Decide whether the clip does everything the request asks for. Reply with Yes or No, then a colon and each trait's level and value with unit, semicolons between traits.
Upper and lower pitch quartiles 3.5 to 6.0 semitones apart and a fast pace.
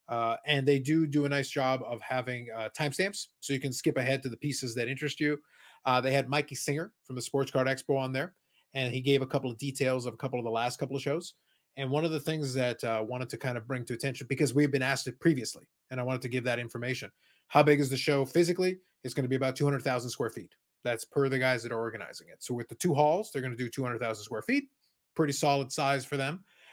No: narrow, 2.5 semitones; fast, 265 wpm